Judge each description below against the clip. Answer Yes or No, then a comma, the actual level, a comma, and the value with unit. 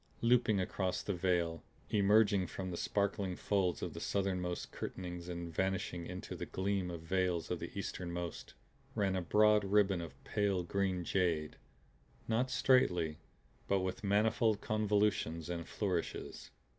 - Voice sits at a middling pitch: No, very low, 95 Hz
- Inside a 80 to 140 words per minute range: Yes, slow, 135 wpm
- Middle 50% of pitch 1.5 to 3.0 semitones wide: Yes, narrow, 2.6 semitones